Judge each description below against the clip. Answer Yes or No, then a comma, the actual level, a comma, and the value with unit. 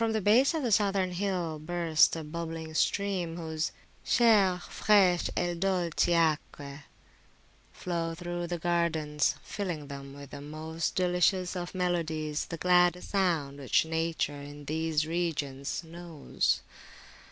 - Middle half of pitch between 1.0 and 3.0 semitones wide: Yes, narrow, 2.5 semitones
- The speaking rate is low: Yes, slow, 130 wpm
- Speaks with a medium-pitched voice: Yes, medium, 170 Hz